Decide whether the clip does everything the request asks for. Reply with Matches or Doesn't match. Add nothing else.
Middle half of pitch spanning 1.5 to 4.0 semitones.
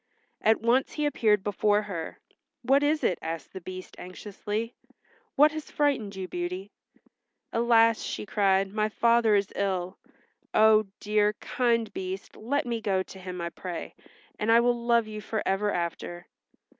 Matches